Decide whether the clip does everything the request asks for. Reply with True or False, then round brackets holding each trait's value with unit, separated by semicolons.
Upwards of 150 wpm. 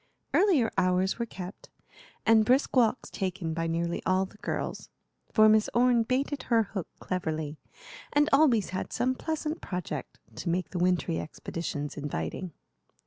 False (145 wpm)